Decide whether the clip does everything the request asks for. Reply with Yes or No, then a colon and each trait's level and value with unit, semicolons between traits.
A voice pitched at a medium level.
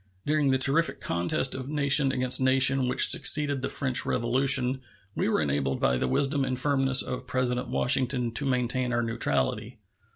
No: low, 130 Hz